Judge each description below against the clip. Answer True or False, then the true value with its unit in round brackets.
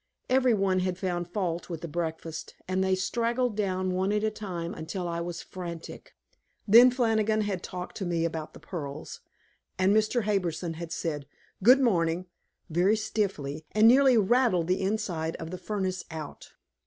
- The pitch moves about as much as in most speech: True (4.1 semitones)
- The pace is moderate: True (165 wpm)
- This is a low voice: False (185 Hz)